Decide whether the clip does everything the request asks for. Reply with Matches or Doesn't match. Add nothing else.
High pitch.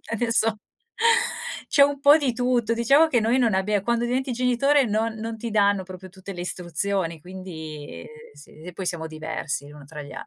Matches